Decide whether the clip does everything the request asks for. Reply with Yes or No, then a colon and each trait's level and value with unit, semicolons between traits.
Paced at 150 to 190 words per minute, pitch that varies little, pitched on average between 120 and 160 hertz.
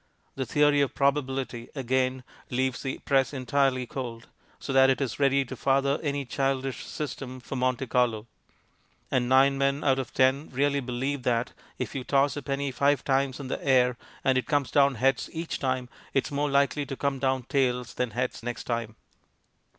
Yes: average, 185 wpm; narrow, 1.6 semitones; low, 135 Hz